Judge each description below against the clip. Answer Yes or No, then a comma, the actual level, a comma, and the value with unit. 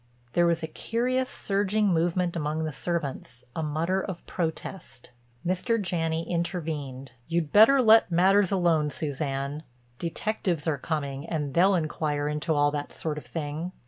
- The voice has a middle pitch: Yes, medium, 165 Hz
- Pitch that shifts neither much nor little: Yes, average, 3.6 semitones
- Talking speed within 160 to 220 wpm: No, average, 145 wpm